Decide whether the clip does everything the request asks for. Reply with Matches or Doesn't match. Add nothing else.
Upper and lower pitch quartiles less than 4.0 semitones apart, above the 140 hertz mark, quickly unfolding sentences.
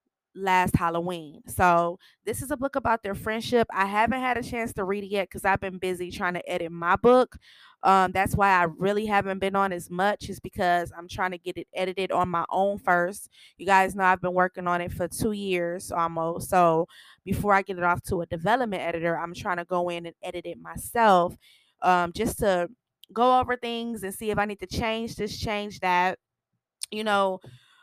Matches